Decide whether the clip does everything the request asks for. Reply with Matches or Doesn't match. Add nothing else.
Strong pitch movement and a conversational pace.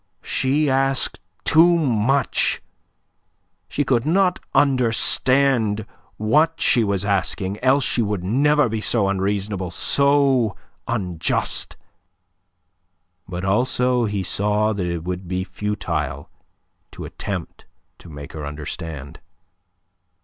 Doesn't match